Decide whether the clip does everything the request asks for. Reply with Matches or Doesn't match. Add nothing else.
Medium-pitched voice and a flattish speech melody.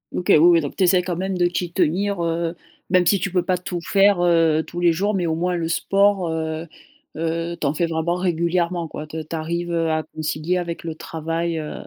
Matches